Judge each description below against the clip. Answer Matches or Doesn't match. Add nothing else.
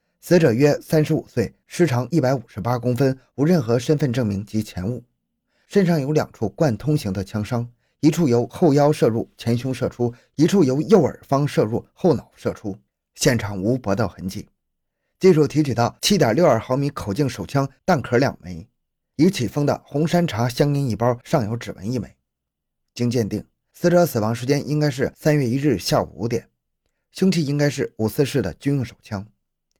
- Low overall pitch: Matches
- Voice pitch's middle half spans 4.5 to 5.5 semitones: Matches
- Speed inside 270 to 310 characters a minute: Matches